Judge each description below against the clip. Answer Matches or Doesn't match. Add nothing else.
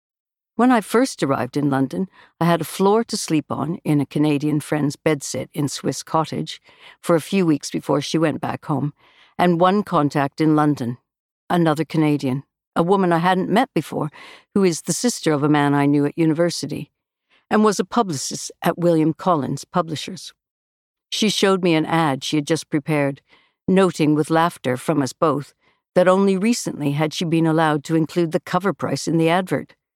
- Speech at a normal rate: Matches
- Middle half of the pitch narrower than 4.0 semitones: Matches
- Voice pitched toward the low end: Doesn't match